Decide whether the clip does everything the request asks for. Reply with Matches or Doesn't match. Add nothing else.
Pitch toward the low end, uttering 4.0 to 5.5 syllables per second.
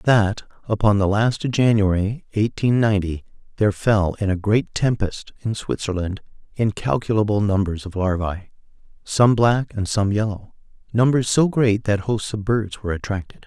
Matches